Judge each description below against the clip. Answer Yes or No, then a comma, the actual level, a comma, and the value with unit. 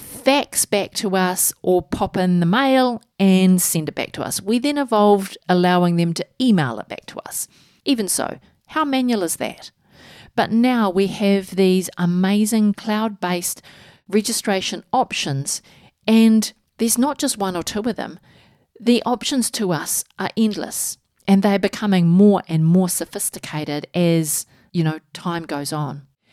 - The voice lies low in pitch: No, high, 195 Hz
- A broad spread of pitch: No, average, 4.4 semitones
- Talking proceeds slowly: No, average, 155 wpm